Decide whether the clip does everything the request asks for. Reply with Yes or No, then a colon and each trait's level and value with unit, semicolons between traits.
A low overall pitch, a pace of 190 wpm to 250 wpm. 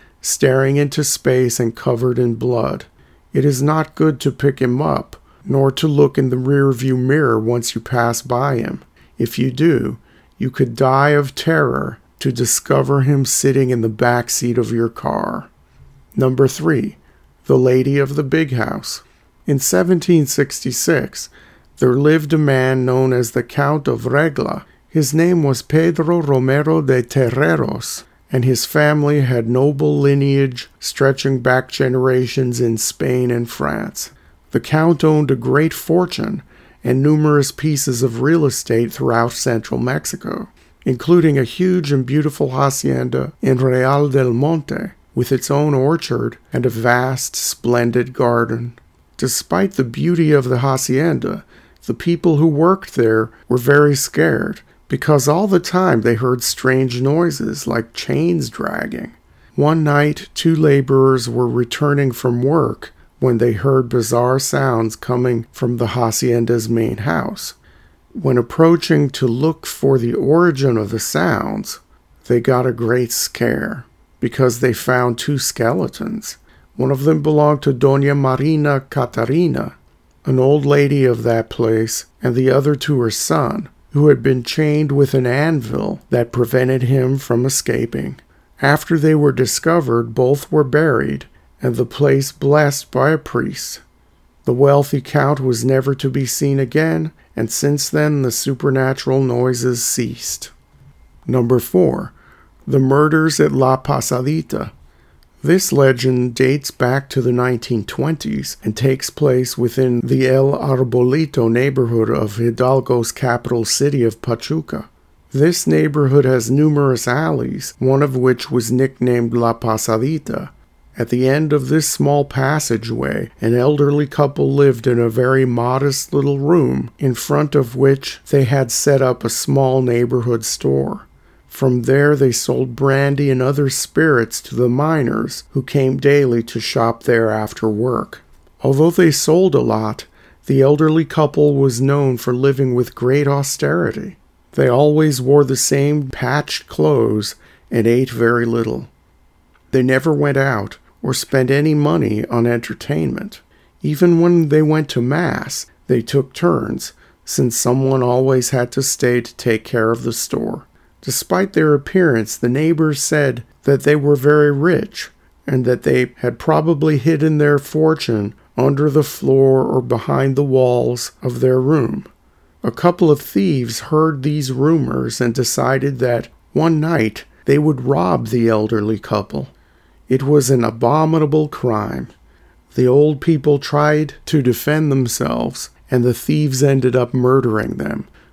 No: low, 130 Hz; average, 145 wpm